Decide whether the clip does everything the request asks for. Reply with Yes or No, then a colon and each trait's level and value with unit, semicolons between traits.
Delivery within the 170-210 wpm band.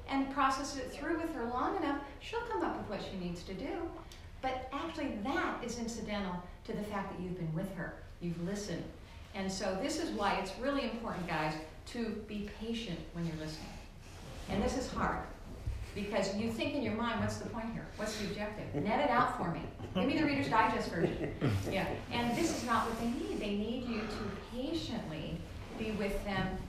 Yes: fast, 205 wpm